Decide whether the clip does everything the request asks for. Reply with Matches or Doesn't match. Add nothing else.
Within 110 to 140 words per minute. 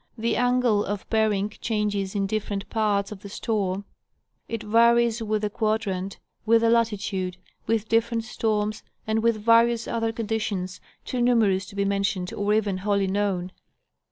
Doesn't match